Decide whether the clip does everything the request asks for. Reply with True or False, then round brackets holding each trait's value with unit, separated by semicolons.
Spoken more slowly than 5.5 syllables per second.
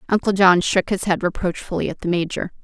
False (5.9 syllables/s)